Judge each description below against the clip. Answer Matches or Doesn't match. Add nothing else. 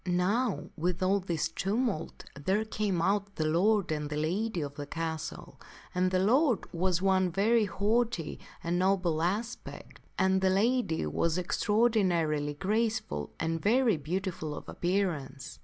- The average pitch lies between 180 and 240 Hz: Matches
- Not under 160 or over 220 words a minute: Doesn't match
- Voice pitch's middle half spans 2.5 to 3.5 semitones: Doesn't match